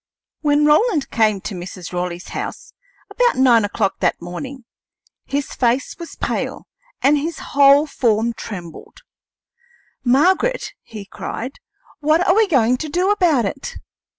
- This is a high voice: Yes, very high, 270 Hz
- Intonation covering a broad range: Yes, wide, 6.3 semitones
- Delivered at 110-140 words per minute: Yes, slow, 135 wpm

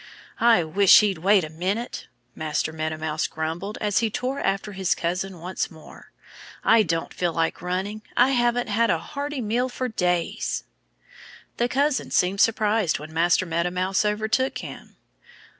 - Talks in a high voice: Yes, high, 195 Hz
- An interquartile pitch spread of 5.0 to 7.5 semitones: Yes, average, 5.3 semitones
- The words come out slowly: No, average, 160 wpm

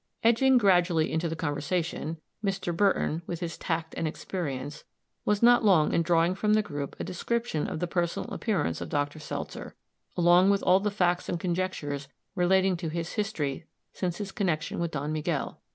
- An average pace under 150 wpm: No, average, 175 wpm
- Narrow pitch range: No, average, 3.6 semitones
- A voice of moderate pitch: Yes, medium, 175 Hz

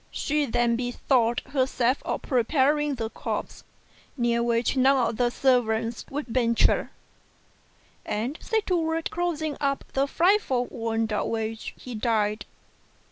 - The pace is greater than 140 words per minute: No, slow, 135 wpm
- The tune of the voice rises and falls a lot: No, average, 3.5 semitones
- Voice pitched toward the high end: Yes, high, 245 Hz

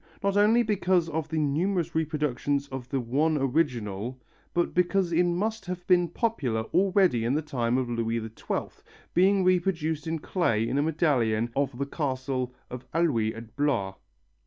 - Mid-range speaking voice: Yes, medium, 150 Hz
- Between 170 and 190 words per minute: No, average, 160 wpm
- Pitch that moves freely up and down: Yes, wide, 6.1 semitones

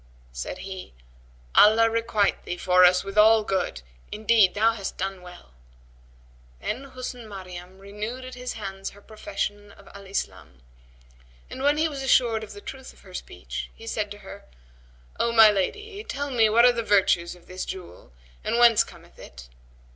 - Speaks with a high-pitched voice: Yes, high, 210 Hz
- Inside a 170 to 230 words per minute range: Yes, average, 175 wpm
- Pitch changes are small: No, average, 3.6 semitones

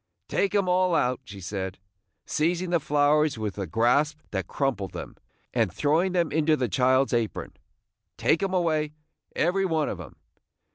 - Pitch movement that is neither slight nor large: No, wide, 6.9 semitones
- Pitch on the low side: No, medium, 145 Hz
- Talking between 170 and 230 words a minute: No, average, 160 wpm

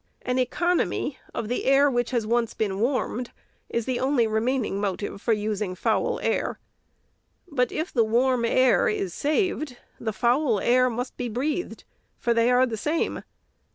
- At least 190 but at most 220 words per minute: No, average, 160 wpm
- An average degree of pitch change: Yes, average, 3.0 semitones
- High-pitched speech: Yes, high, 245 Hz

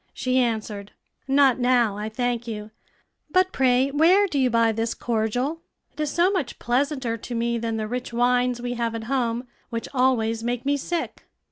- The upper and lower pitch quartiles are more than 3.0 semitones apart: No, average, 2.7 semitones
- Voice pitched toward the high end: Yes, high, 245 Hz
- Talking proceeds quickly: No, average, 180 wpm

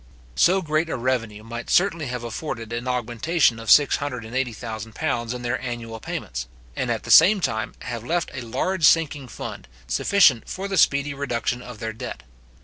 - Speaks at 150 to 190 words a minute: Yes, average, 165 wpm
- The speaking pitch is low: Yes, low, 125 Hz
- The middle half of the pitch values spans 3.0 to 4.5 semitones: No, average, 5.1 semitones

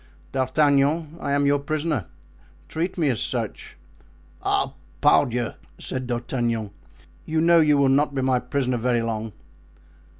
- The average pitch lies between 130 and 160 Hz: Yes, low, 135 Hz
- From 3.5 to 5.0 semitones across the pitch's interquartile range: Yes, average, 3.9 semitones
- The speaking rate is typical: No, slow, 130 wpm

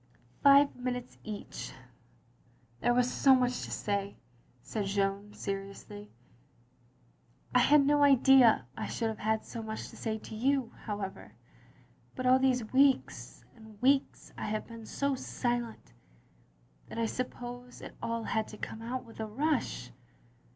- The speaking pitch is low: No, high, 230 Hz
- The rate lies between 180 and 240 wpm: No, average, 150 wpm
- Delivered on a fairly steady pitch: No, average, 3.4 semitones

